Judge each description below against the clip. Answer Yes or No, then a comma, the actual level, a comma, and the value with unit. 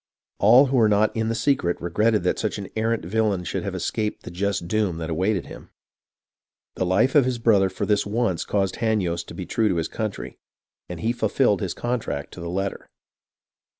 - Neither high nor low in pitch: No, low, 105 Hz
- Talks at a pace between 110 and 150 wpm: No, average, 200 wpm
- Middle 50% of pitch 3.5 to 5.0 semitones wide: Yes, average, 3.8 semitones